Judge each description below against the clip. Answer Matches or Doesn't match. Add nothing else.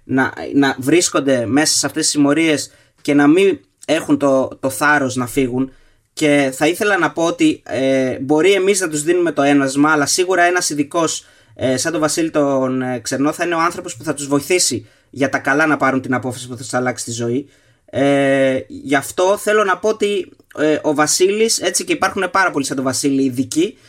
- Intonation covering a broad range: Doesn't match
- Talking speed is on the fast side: Matches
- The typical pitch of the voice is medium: Matches